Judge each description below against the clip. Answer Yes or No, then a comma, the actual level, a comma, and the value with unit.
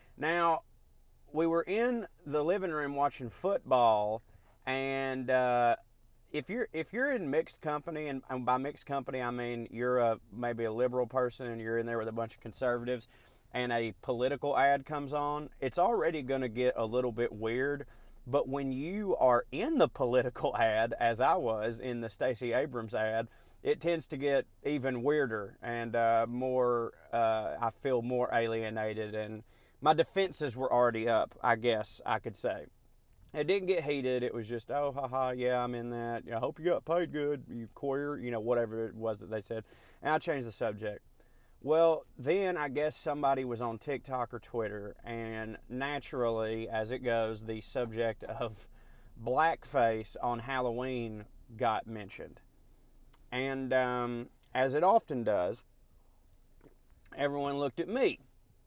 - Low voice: Yes, low, 125 Hz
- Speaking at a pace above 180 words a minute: No, average, 165 wpm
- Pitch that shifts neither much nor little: Yes, average, 3.7 semitones